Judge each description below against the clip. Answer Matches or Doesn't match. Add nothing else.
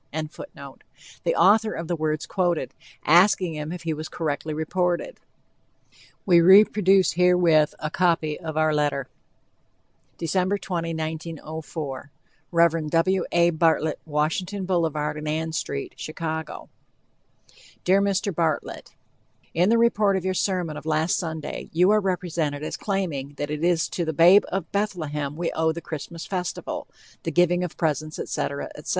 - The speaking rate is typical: Matches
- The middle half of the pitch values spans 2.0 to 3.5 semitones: Matches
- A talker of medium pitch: Matches